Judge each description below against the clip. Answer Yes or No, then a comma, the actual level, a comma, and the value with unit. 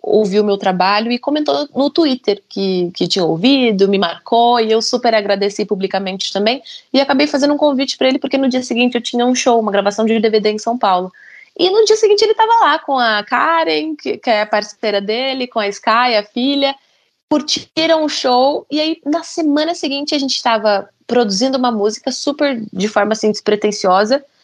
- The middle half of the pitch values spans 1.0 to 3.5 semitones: No, average, 5.3 semitones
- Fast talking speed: Yes, fast, 200 wpm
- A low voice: No, high, 240 Hz